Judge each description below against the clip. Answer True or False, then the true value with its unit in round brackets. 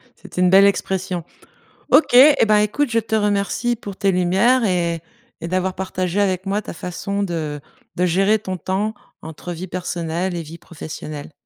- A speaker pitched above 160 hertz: True (185 Hz)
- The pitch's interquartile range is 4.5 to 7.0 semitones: False (2.9 semitones)